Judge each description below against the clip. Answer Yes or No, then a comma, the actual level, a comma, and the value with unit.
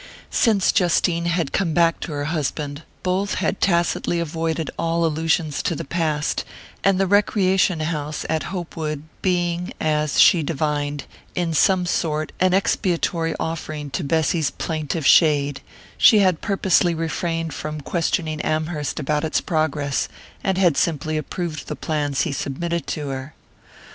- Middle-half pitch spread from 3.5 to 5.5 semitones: No, narrow, 2.5 semitones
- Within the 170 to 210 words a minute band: No, average, 145 wpm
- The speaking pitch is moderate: Yes, medium, 160 Hz